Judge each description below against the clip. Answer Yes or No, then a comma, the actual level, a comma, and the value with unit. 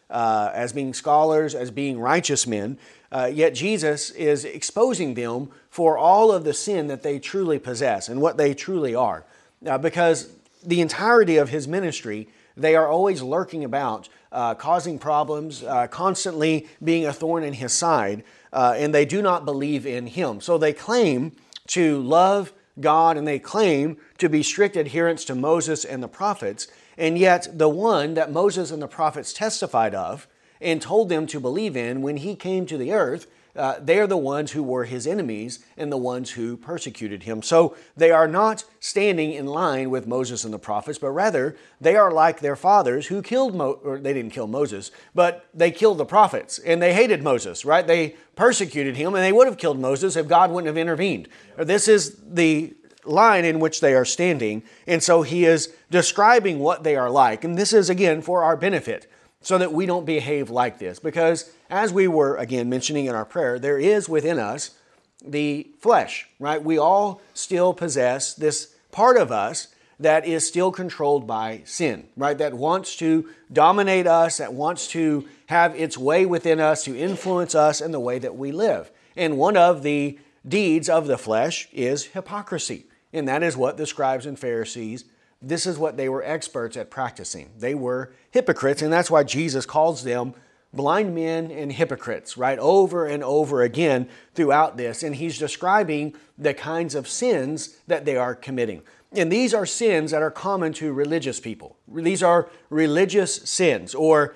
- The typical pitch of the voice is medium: Yes, medium, 155 Hz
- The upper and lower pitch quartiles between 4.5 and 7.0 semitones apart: No, average, 3.9 semitones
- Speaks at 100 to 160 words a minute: No, average, 185 wpm